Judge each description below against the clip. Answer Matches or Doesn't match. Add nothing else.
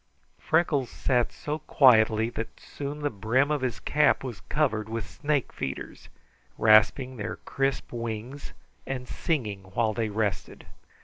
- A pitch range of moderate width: Matches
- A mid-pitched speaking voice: Doesn't match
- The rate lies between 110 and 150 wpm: Matches